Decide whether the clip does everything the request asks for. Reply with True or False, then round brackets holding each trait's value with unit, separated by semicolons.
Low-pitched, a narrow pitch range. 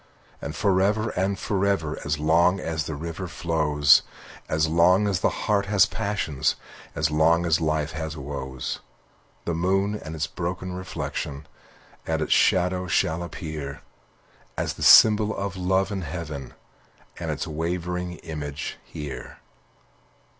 False (85 Hz; 3.5 semitones)